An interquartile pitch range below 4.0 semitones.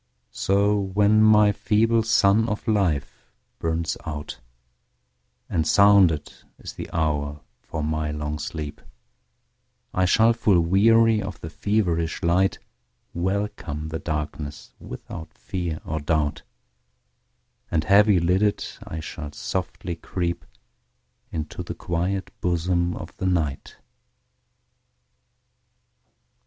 No: average, 4.6 semitones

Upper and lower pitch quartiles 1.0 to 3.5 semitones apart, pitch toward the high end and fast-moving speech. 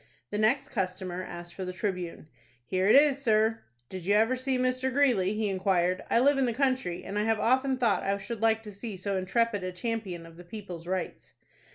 No: average, 4.7 semitones; high, 210 Hz; fast, 215 wpm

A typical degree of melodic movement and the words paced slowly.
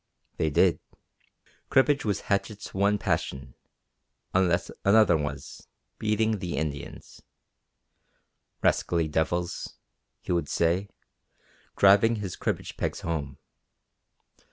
Yes: average, 4.2 semitones; slow, 95 wpm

